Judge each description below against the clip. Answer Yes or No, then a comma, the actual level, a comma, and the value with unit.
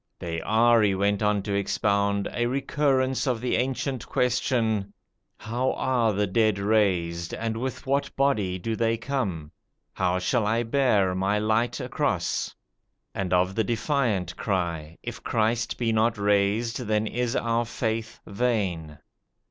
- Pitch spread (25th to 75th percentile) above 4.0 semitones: No, average, 3.4 semitones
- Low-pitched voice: Yes, low, 110 Hz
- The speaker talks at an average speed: Yes, average, 145 wpm